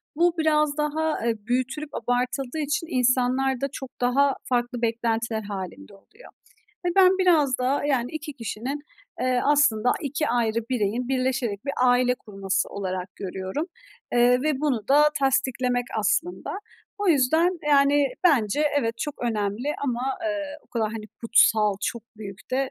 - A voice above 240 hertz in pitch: Yes, very high, 255 Hz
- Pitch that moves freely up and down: No, average, 4.2 semitones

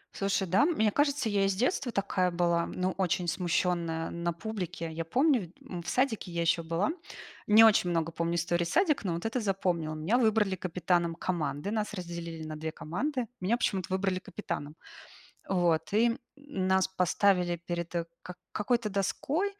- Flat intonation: No, average, 4.0 semitones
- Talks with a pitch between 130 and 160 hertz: No, medium, 185 Hz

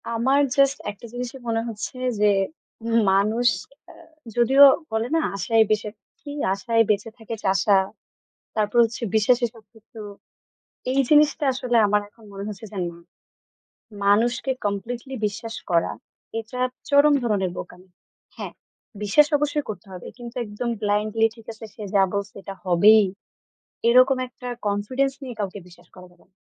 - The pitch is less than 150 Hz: No, high, 225 Hz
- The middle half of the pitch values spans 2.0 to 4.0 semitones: Yes, average, 3.4 semitones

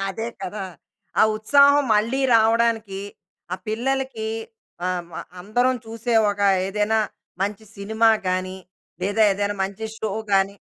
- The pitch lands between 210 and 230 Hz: Yes, high, 215 Hz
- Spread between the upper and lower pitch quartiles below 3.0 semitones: Yes, narrow, 2.6 semitones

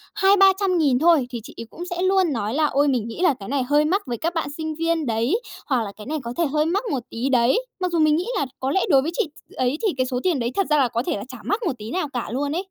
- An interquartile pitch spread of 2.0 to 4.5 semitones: No, wide, 5.6 semitones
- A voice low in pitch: No, very high, 295 Hz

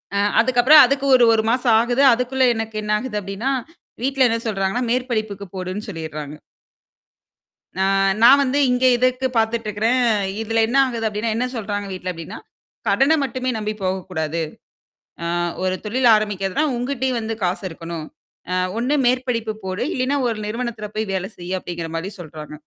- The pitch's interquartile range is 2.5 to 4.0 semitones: No, average, 4.7 semitones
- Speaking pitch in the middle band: No, high, 225 Hz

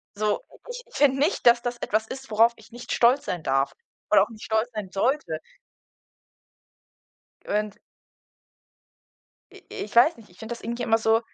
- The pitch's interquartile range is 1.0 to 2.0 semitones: No, narrow, 2.4 semitones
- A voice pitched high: Yes, high, 230 Hz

